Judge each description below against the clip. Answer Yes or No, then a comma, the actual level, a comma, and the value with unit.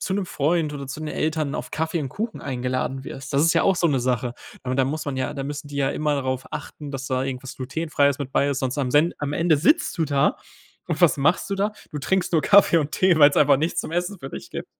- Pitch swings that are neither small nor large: Yes, average, 3.4 semitones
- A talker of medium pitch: Yes, medium, 145 Hz